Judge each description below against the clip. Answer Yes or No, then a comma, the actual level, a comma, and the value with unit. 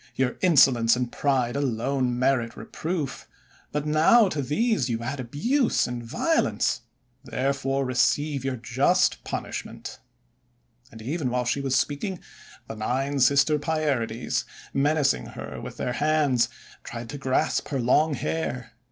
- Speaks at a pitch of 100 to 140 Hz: Yes, low, 135 Hz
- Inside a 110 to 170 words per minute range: Yes, slow, 135 wpm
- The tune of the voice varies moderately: Yes, average, 3.4 semitones